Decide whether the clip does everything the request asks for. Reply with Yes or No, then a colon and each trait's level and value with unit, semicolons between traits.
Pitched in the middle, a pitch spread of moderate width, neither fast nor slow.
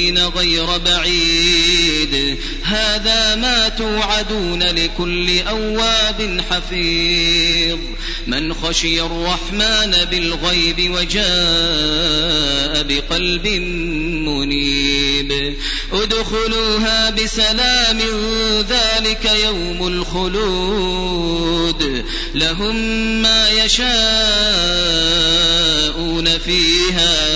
No: medium, 175 Hz; average, 4.5 semitones; slow, 55 wpm